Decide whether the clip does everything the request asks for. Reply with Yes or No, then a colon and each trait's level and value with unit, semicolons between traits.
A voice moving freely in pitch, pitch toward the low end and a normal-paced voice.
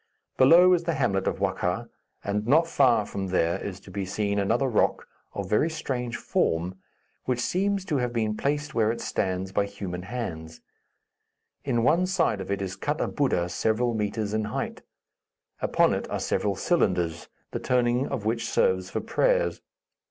Yes: wide, 6.1 semitones; low, 110 Hz; average, 175 wpm